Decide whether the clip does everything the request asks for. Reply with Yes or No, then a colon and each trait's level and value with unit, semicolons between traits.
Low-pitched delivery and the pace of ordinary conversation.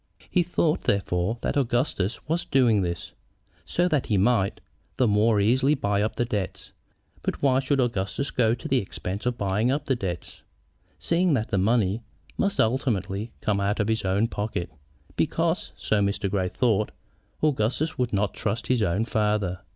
Yes: low, 110 Hz; average, 170 wpm